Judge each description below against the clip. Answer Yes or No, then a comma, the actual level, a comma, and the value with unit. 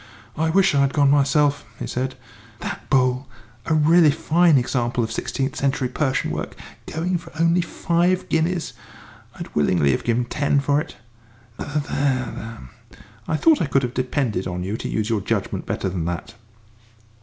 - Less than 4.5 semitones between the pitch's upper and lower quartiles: No, average, 4.8 semitones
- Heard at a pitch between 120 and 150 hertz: Yes, medium, 140 Hz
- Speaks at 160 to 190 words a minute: Yes, average, 165 wpm